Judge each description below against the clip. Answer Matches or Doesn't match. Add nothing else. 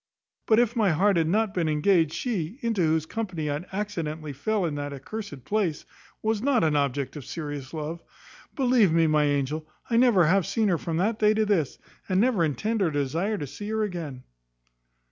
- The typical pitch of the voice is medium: Matches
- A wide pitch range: Matches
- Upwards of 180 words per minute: Matches